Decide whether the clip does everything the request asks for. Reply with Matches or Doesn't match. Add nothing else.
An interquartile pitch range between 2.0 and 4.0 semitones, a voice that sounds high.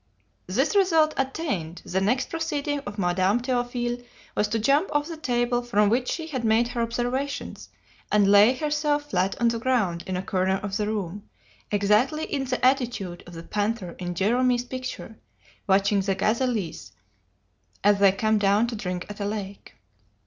Doesn't match